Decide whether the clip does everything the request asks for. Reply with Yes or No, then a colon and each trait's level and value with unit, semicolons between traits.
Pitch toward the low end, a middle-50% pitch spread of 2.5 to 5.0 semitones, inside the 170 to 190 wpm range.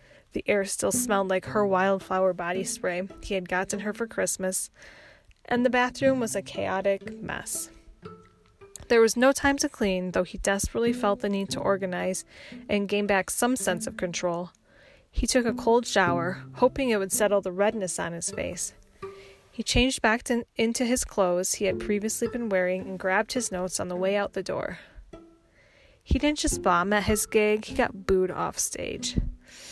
No: high, 205 Hz; average, 4.2 semitones; average, 185 wpm